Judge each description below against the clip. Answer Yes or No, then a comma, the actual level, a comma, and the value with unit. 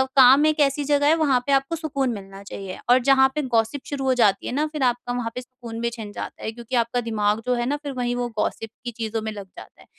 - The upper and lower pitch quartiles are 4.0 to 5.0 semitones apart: No, average, 3.5 semitones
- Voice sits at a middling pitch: No, high, 245 Hz